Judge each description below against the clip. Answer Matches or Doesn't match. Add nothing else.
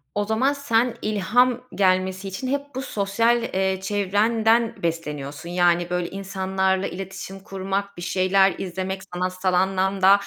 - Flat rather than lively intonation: Matches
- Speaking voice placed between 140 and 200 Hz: Matches